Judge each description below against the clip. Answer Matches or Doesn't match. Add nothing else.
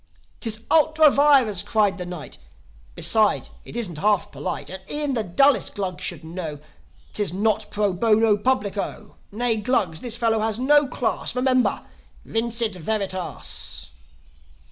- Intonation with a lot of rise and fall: Doesn't match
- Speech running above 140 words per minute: Doesn't match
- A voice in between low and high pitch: Doesn't match